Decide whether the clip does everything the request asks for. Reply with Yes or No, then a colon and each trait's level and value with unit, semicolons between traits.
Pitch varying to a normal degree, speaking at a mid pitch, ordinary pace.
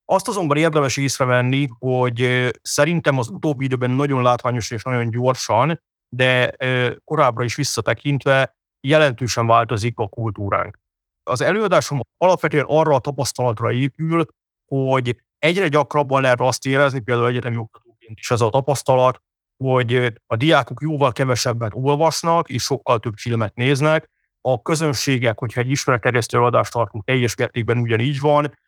No: average, 3.1 semitones; low, 130 Hz; average, 135 wpm